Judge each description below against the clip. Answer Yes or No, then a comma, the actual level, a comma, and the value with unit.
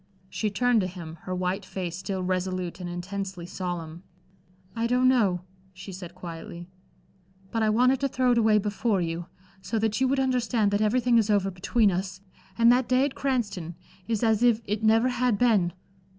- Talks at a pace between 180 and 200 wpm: Yes, average, 185 wpm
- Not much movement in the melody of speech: No, average, 4.5 semitones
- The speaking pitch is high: Yes, high, 205 Hz